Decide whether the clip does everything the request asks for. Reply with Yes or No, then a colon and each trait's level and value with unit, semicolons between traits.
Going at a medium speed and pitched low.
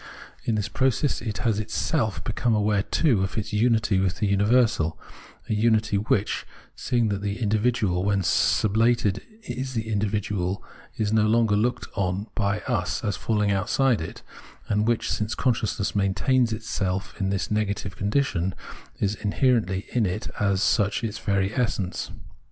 Yes: average, 160 wpm; low, 105 Hz